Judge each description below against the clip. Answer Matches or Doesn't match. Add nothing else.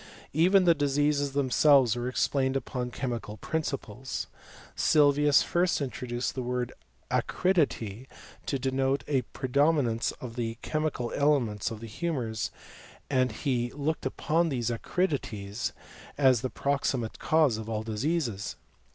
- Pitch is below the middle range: Matches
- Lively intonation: Doesn't match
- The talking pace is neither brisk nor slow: Doesn't match